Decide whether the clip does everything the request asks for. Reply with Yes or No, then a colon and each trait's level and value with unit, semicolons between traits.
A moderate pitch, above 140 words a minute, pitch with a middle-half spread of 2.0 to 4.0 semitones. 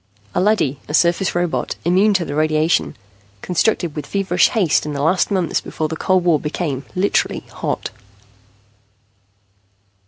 No: medium, 170 Hz; slow, 135 wpm; average, 3.5 semitones